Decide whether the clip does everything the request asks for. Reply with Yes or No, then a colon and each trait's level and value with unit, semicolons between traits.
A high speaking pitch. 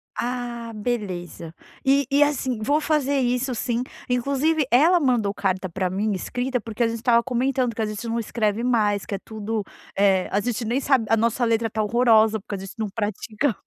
Yes: high, 230 Hz